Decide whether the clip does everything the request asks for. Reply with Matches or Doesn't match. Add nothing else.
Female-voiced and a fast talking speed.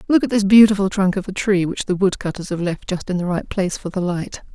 Matches